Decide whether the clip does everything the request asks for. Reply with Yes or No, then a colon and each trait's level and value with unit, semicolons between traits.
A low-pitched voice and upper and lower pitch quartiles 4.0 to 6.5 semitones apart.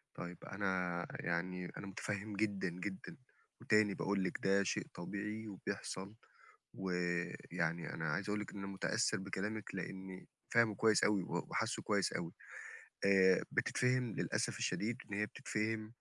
No: low, 100 Hz; narrow, 2.5 semitones